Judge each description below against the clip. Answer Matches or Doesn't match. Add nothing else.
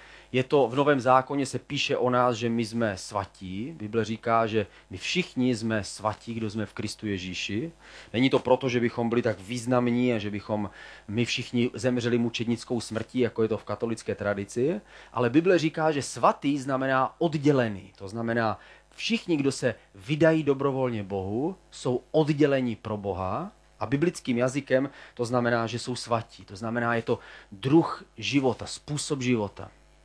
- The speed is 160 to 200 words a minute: Matches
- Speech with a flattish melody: Doesn't match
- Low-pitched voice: Matches